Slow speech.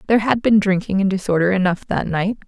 No: fast, 220 wpm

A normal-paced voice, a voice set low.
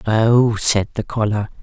Yes: average, 150 wpm; low, 110 Hz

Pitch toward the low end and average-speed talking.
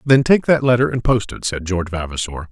No: low, 110 Hz; fast, 240 wpm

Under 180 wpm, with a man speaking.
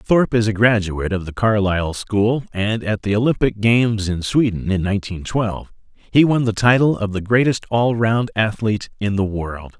No: average, 190 wpm; male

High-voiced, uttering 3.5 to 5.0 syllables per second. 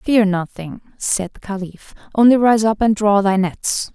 Yes: high, 205 Hz; 4.2 syllables/s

